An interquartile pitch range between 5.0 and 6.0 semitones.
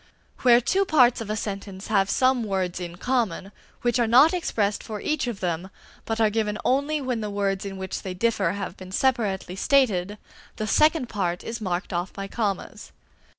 No: average, 4.2 semitones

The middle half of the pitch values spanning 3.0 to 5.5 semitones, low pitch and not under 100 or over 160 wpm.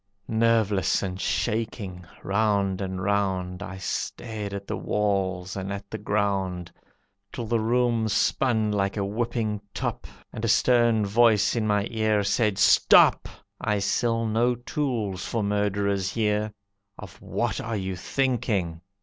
No: narrow, 2.5 semitones; low, 105 Hz; average, 140 wpm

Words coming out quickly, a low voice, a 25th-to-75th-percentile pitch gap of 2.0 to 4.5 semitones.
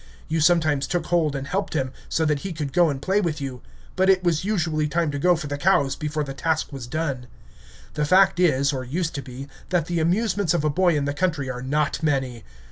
No: fast, 235 wpm; medium, 155 Hz; average, 3.8 semitones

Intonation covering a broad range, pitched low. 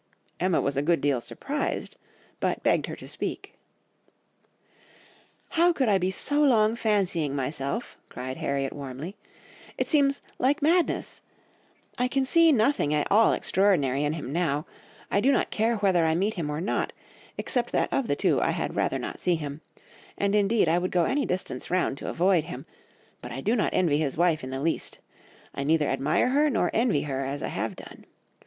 No: wide, 8.0 semitones; medium, 180 Hz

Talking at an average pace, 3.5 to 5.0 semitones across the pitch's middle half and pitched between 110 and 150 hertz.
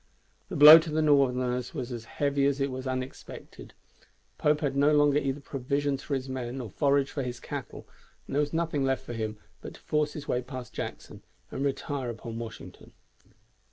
No: average, 190 wpm; narrow, 2.5 semitones; low, 135 Hz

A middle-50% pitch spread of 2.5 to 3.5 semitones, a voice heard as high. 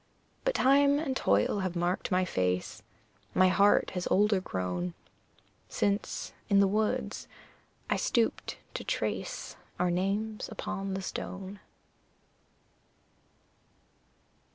Yes: average, 2.9 semitones; high, 195 Hz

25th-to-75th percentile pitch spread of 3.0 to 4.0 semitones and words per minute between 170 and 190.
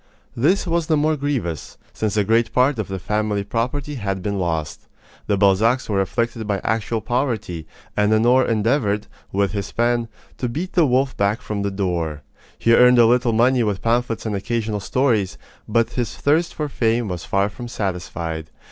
Yes: average, 3.7 semitones; average, 180 wpm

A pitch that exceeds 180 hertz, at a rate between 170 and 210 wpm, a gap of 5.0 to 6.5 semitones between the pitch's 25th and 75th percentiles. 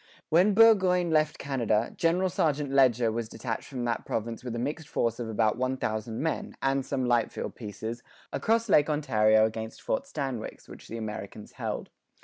No: low, 125 Hz; average, 175 wpm; wide, 5.5 semitones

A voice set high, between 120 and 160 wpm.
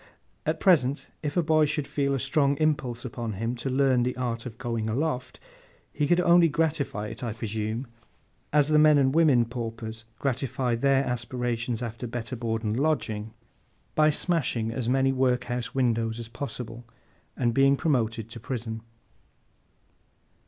No: low, 125 Hz; average, 155 wpm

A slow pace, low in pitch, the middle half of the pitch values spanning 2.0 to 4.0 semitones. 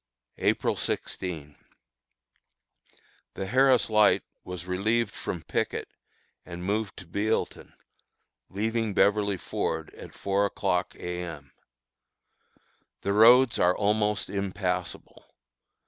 Yes: slow, 100 wpm; low, 100 Hz; average, 3.1 semitones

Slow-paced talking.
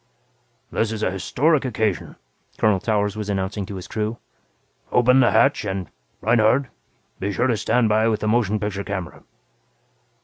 No: average, 160 wpm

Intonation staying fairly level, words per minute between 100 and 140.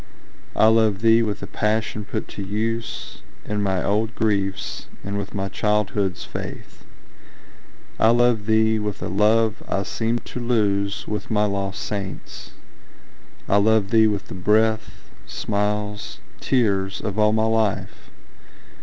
Yes: narrow, 1.7 semitones; slow, 135 wpm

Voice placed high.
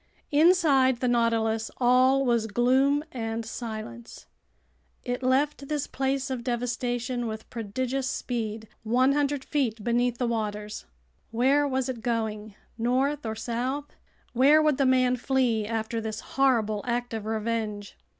Yes: high, 245 Hz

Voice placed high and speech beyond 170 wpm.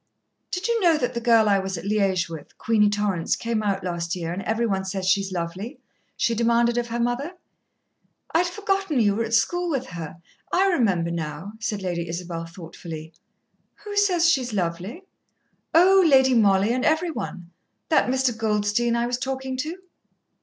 Yes: high, 225 Hz; average, 180 wpm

